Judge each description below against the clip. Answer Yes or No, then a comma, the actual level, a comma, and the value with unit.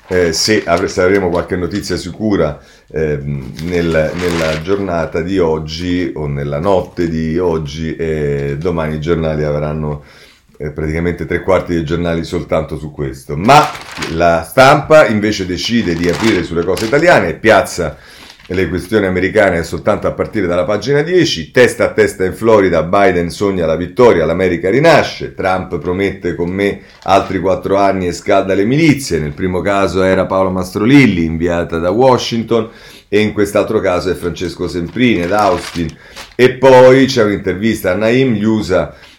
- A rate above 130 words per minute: Yes, average, 155 wpm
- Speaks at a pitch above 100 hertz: No, very low, 90 Hz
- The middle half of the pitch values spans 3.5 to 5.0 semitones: Yes, average, 3.8 semitones